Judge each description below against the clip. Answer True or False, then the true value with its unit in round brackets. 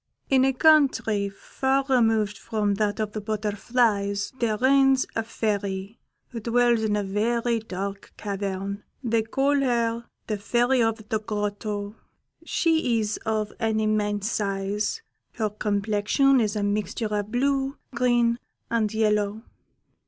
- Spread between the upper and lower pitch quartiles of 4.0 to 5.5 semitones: False (2.7 semitones)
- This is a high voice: True (220 Hz)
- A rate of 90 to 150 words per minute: True (135 wpm)